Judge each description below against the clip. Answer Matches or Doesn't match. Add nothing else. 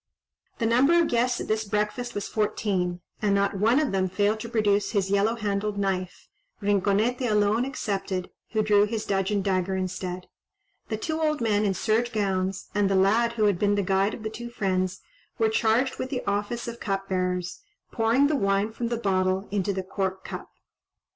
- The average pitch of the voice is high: Matches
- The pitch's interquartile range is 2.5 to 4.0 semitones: Matches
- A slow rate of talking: Doesn't match